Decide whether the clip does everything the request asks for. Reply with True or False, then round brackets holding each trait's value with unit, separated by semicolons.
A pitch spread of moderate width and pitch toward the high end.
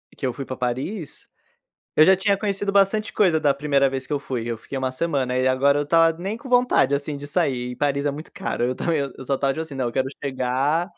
False (4.2 semitones; 140 Hz)